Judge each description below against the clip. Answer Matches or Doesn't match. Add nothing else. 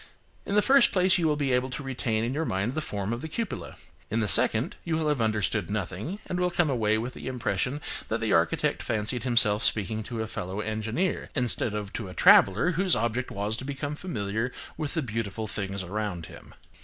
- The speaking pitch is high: Doesn't match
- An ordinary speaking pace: Doesn't match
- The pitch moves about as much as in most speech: Doesn't match